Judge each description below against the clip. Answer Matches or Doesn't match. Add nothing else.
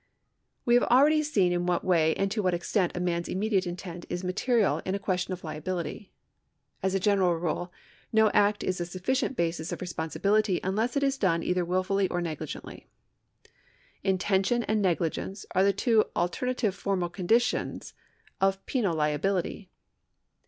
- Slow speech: Doesn't match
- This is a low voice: Doesn't match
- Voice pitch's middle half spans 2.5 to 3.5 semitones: Matches